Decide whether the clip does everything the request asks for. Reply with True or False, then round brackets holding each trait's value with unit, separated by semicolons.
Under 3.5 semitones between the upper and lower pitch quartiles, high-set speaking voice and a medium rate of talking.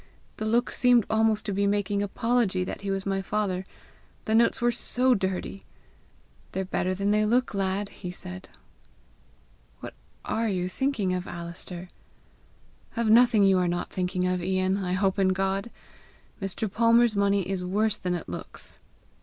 True (2.8 semitones; 195 Hz; 160 wpm)